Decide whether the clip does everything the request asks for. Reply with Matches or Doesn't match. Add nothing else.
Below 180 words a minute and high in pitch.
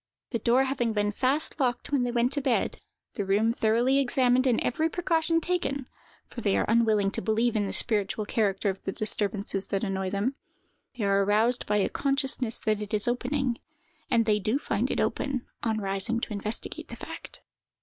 Doesn't match